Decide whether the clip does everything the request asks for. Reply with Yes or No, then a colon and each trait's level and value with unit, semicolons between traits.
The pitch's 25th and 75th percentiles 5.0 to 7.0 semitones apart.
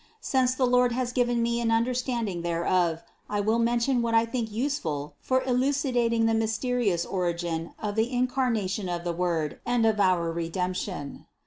Yes: wide, 5.5 semitones